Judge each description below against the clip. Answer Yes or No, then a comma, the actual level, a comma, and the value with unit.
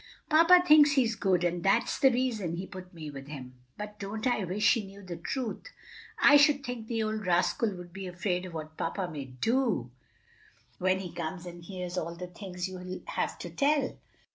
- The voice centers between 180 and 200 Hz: Yes, high, 190 Hz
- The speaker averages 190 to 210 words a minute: Yes, average, 200 wpm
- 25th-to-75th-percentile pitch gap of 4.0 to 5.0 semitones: Yes, average, 4.7 semitones